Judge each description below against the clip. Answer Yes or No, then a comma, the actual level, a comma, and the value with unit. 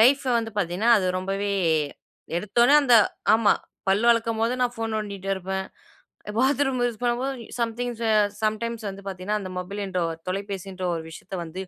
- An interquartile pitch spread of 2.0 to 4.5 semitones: Yes, average, 3.7 semitones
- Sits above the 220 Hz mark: No, high, 210 Hz